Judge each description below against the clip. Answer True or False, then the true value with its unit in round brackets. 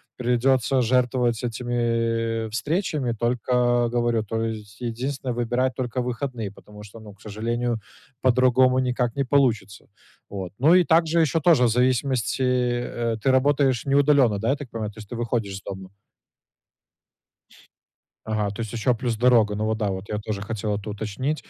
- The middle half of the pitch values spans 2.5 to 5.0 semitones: True (2.8 semitones)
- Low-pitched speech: True (120 Hz)